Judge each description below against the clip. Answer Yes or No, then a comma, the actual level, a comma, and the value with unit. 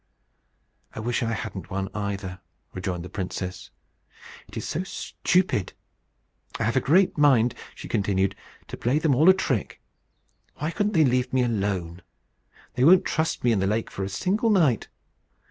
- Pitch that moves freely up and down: Yes, wide, 7.9 semitones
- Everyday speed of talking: Yes, average, 165 wpm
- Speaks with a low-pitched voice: Yes, low, 115 Hz